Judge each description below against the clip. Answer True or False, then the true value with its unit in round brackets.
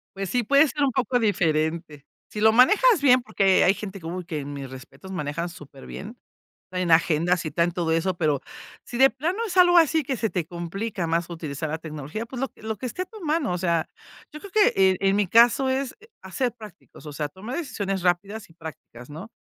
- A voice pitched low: False (190 Hz)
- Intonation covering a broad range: True (7.3 semitones)